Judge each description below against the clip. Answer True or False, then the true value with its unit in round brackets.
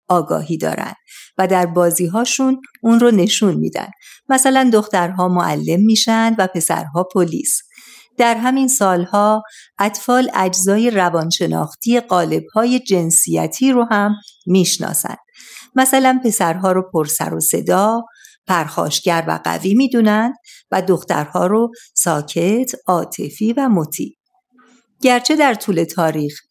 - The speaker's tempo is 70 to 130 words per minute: True (110 wpm)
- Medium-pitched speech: False (210 Hz)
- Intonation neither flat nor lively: False (5.7 semitones)